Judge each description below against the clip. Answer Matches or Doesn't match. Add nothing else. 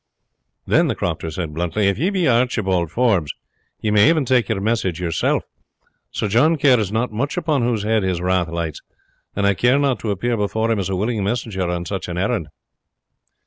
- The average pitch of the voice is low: Matches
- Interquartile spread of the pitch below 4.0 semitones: Doesn't match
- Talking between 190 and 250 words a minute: Matches